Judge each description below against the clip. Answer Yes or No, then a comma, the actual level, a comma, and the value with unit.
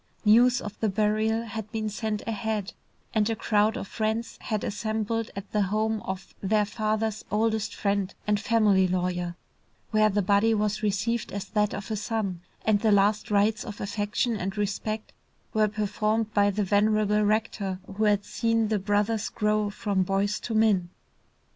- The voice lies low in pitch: No, high, 210 Hz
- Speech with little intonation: Yes, narrow, 1.3 semitones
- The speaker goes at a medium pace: Yes, average, 165 wpm